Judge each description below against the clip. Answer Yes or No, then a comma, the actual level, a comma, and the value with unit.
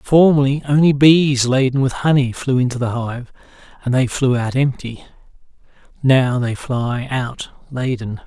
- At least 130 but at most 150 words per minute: Yes, average, 145 wpm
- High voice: No, low, 130 Hz